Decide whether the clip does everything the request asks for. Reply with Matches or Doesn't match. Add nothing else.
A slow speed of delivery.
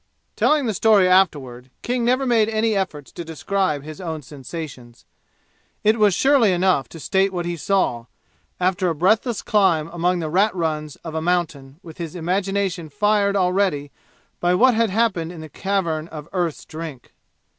Doesn't match